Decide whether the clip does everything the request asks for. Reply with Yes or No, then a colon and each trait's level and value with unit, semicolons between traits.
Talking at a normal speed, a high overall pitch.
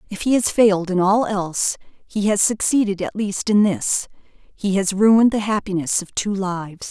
Yes: average, 190 wpm; high, 200 Hz